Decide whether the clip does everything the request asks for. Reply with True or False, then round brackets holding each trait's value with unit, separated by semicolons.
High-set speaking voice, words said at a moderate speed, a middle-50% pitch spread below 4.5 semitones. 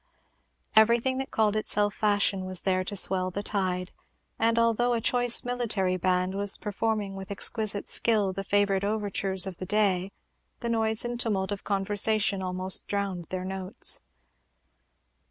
True (200 Hz; 150 wpm; 2.6 semitones)